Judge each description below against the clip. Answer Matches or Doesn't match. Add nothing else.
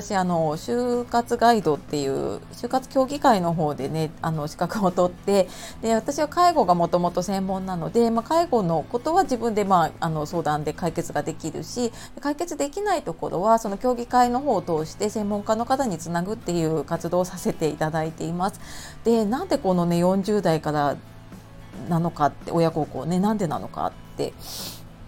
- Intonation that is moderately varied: Doesn't match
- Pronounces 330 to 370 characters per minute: Matches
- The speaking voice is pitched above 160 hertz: Matches